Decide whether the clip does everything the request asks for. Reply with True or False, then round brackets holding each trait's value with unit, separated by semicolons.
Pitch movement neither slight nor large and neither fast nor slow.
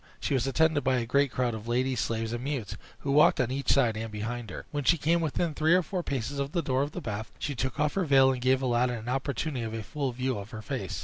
False (3.4 semitones; 275 wpm)